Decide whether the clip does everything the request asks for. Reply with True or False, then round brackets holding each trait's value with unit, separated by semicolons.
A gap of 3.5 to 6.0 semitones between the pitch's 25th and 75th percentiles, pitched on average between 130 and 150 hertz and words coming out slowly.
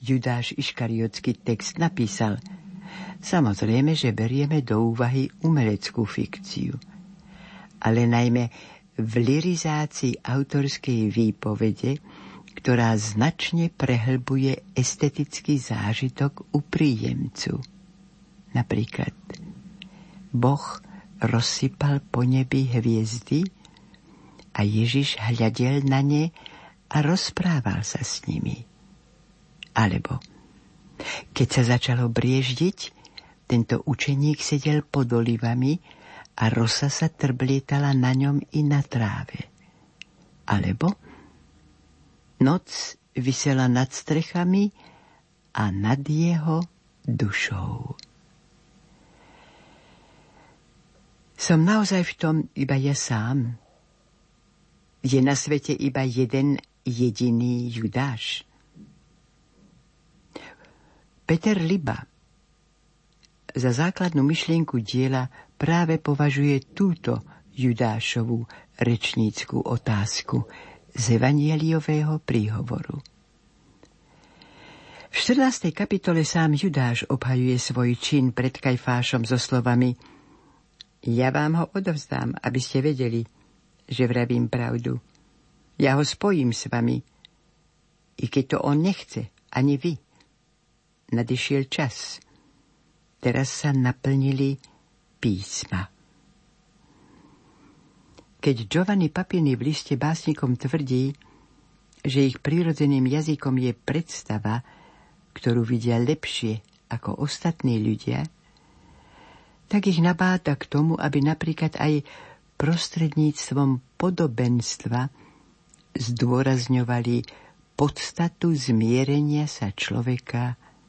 True (4.3 semitones; 135 Hz; 85 wpm)